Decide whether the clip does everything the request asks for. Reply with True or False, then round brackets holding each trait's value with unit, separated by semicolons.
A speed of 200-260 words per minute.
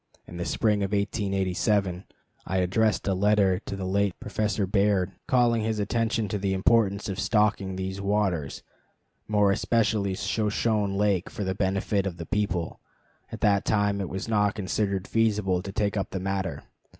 False (165 wpm)